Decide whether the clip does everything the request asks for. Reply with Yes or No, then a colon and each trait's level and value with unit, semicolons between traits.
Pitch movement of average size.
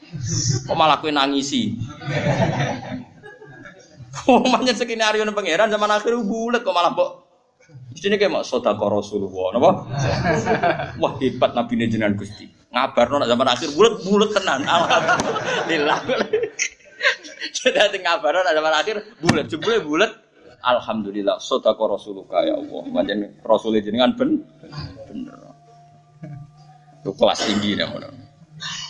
No: wide, 8.4 semitones